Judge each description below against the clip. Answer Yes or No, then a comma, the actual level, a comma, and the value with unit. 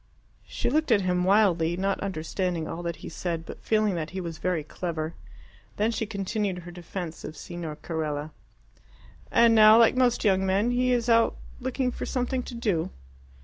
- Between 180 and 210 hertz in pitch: Yes, high, 190 Hz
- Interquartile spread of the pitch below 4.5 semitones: No, average, 5.1 semitones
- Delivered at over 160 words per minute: Yes, average, 180 wpm